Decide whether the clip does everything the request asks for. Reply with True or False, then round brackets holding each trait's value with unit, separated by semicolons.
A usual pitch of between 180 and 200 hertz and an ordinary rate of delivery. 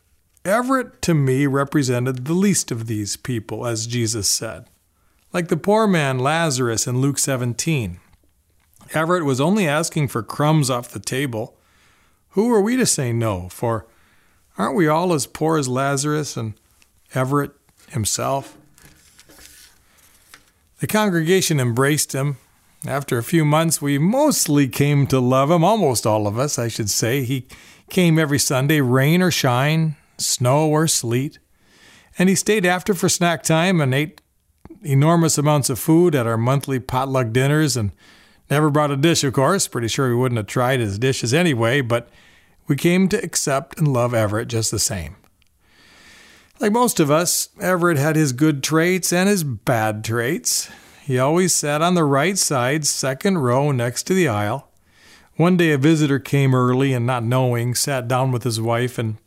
False (140 Hz; 165 wpm)